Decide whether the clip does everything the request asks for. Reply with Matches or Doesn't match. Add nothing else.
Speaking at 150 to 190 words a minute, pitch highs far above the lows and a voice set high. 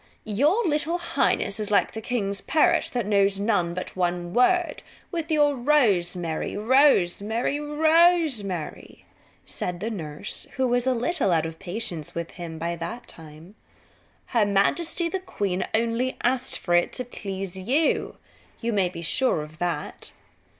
Doesn't match